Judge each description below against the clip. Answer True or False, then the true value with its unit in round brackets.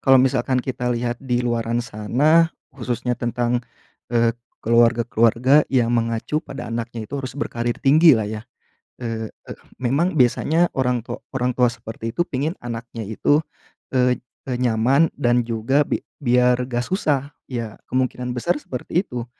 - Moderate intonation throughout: False (2.3 semitones)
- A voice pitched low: True (125 Hz)